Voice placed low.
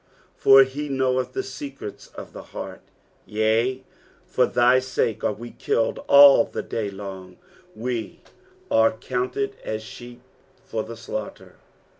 Yes: low, 120 Hz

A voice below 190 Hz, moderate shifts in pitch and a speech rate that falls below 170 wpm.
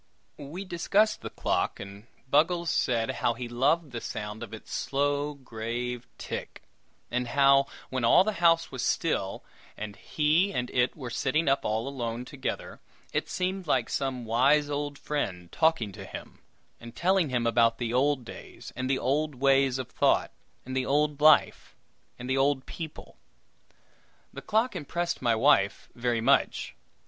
Yes: low, 135 Hz; average, 4.0 semitones; average, 160 wpm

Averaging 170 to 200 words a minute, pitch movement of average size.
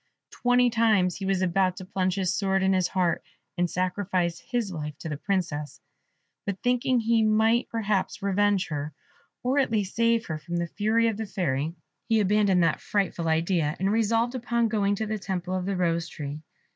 Yes: average, 190 wpm; average, 4.0 semitones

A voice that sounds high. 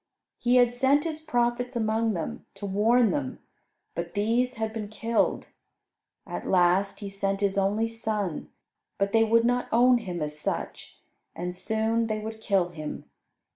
Yes: high, 220 Hz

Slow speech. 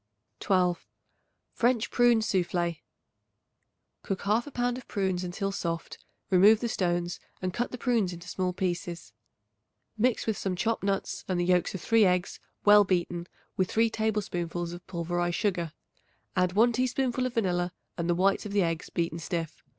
No: average, 160 wpm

